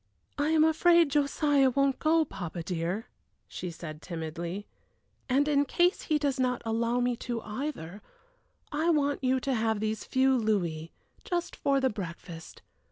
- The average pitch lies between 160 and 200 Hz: No, very high, 255 Hz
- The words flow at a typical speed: Yes, average, 155 wpm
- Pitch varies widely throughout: Yes, wide, 6.9 semitones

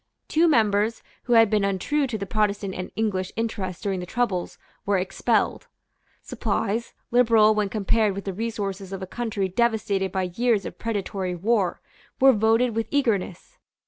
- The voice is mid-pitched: No, high, 210 Hz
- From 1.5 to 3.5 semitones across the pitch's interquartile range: Yes, average, 3.0 semitones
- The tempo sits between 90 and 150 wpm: No, average, 160 wpm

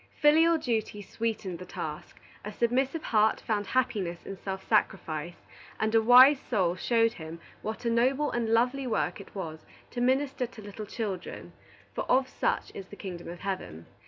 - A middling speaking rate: Yes, average, 170 wpm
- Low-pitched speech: No, high, 220 Hz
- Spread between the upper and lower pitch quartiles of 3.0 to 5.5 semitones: Yes, average, 4.7 semitones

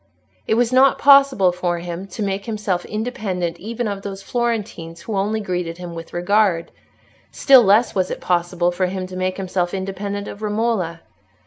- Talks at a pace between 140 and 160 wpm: No, average, 175 wpm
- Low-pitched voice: No, high, 195 Hz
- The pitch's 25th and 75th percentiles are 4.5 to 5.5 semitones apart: No, average, 3.5 semitones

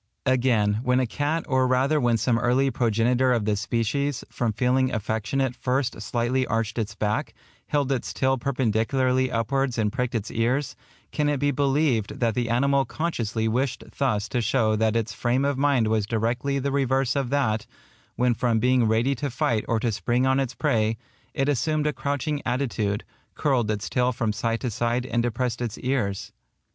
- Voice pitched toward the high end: No, low, 125 Hz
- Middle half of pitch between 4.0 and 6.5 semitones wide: No, average, 3.0 semitones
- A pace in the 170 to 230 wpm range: Yes, average, 180 wpm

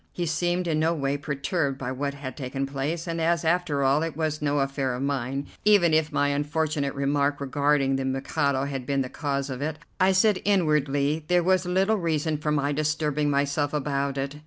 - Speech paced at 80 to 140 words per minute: No, average, 200 wpm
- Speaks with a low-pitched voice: No, medium, 145 Hz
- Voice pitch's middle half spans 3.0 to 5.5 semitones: No, narrow, 2.6 semitones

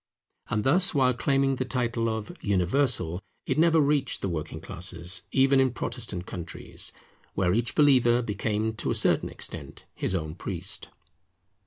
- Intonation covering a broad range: Yes, wide, 6.5 semitones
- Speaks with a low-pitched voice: Yes, low, 110 Hz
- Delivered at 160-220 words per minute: No, average, 150 wpm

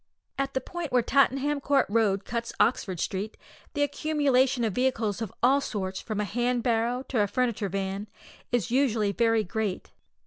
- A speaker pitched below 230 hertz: No, high, 235 Hz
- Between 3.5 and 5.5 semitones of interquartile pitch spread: Yes, average, 4.1 semitones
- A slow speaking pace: No, average, 170 wpm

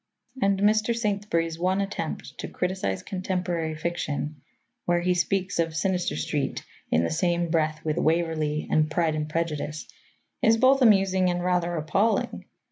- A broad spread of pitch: No, average, 3.4 semitones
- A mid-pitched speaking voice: Yes, medium, 175 Hz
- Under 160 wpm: Yes, average, 145 wpm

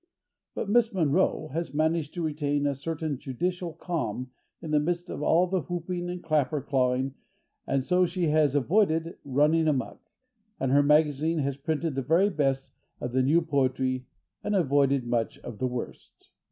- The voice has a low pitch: No, medium, 150 Hz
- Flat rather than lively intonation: No, average, 3.8 semitones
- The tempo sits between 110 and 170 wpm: Yes, average, 165 wpm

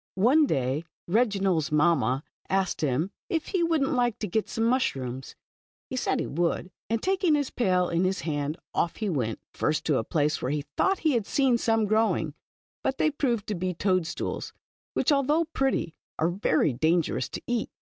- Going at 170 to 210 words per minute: Yes, average, 195 wpm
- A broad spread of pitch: Yes, wide, 8.1 semitones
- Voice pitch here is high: Yes, high, 195 Hz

